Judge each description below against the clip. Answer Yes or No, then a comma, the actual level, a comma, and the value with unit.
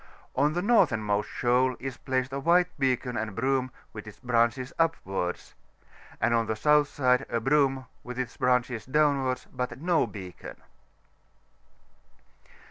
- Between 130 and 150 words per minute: Yes, slow, 135 wpm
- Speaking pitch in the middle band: No, low, 130 Hz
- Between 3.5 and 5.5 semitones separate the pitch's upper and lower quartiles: No, average, 2.9 semitones